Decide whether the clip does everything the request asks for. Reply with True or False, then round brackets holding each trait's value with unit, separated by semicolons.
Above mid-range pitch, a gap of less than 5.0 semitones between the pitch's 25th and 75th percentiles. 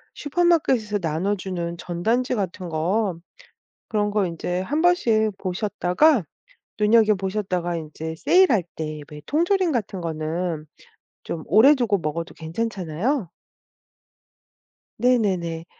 False (195 Hz; 5.3 semitones)